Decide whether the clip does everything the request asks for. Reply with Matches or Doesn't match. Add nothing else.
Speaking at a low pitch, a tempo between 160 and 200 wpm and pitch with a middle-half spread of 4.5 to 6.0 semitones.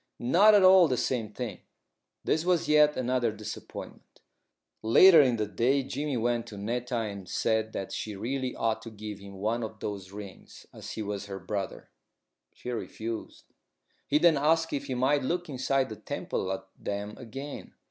Matches